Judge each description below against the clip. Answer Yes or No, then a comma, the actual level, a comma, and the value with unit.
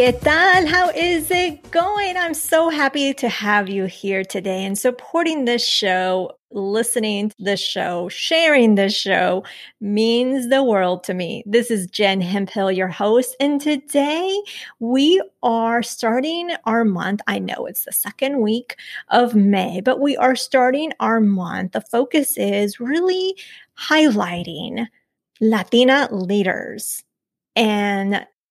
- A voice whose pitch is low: No, high, 235 Hz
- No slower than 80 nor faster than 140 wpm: Yes, slow, 135 wpm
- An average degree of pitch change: No, wide, 6.2 semitones